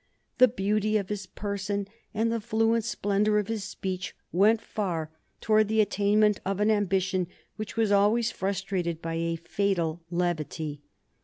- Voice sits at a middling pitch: No, high, 200 Hz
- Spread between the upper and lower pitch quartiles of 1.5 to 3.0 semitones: Yes, average, 2.7 semitones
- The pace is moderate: Yes, average, 150 wpm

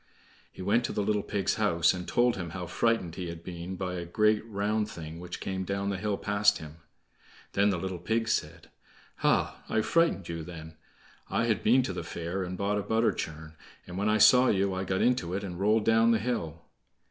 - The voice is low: Yes, very low, 95 Hz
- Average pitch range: Yes, average, 3.6 semitones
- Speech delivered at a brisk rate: Yes, fast, 215 wpm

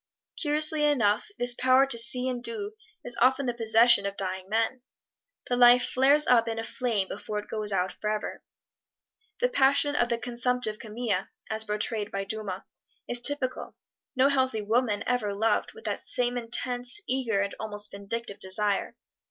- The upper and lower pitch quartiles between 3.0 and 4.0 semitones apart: Yes, average, 3.4 semitones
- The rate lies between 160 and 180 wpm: Yes, average, 165 wpm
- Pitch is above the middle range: Yes, high, 235 Hz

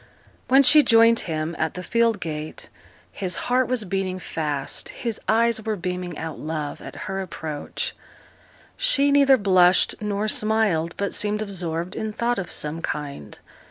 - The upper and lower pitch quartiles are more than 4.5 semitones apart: Yes, wide, 5.6 semitones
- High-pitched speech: Yes, high, 195 Hz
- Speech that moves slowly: No, average, 155 wpm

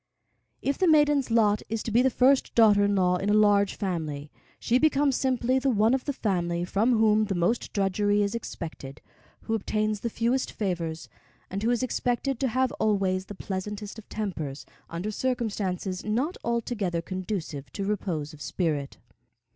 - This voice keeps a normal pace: Yes, average, 170 wpm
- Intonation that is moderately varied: Yes, average, 4.3 semitones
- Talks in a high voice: Yes, high, 210 Hz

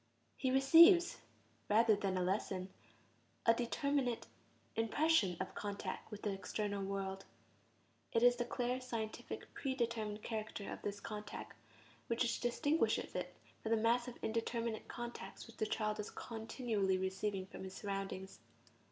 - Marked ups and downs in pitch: No, average, 3.3 semitones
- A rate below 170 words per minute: Yes, average, 140 wpm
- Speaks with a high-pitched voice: Yes, high, 220 Hz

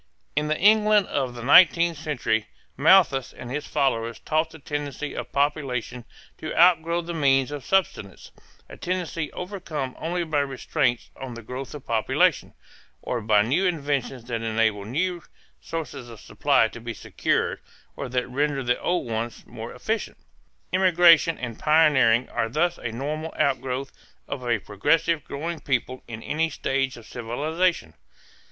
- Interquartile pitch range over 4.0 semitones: Yes, average, 5.0 semitones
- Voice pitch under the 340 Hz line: Yes, medium, 140 Hz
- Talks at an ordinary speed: Yes, average, 150 wpm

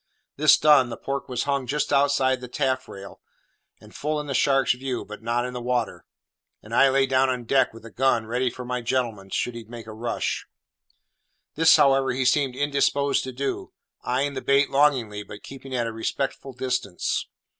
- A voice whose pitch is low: Yes, low, 130 Hz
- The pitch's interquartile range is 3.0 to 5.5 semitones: No, narrow, 2.4 semitones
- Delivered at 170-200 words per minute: Yes, average, 190 wpm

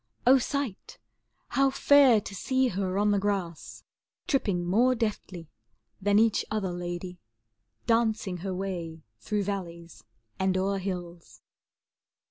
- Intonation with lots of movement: No, average, 3.8 semitones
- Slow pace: Yes, slow, 120 wpm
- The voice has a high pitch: Yes, high, 195 Hz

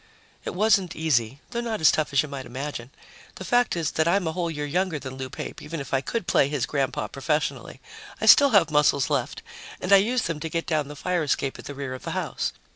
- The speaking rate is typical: No, fast, 245 wpm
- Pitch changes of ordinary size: Yes, average, 4.5 semitones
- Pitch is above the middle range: No, medium, 150 Hz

